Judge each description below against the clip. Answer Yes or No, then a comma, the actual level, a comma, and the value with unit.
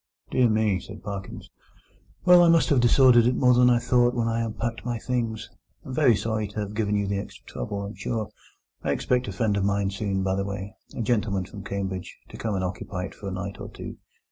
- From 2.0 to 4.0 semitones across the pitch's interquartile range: Yes, average, 3.3 semitones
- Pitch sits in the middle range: No, low, 105 Hz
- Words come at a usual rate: No, fast, 220 wpm